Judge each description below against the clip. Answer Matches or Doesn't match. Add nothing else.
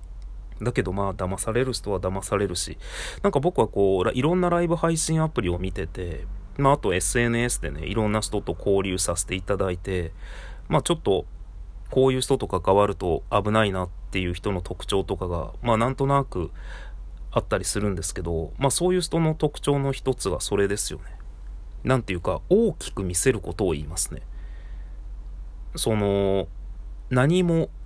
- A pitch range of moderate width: Doesn't match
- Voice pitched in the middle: Doesn't match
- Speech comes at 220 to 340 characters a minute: Matches